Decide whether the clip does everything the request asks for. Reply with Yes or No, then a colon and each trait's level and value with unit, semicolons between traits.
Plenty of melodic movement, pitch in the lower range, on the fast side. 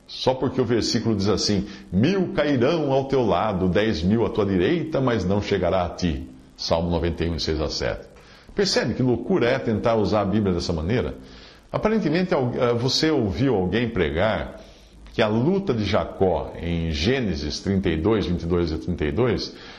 No: wide, 7.0 semitones; low, 105 Hz; average, 155 wpm